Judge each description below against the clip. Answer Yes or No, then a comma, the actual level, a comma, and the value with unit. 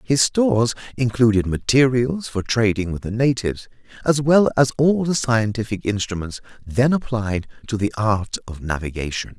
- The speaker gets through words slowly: No, average, 145 wpm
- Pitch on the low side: Yes, low, 115 Hz